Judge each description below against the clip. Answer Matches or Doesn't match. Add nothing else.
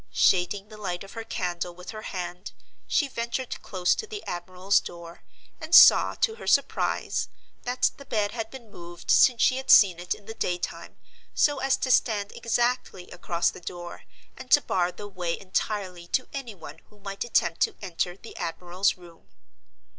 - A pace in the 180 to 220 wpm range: Matches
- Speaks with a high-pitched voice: Matches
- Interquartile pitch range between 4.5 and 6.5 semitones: Matches